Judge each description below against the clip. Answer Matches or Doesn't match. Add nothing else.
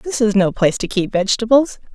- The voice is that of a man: Doesn't match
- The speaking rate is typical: Doesn't match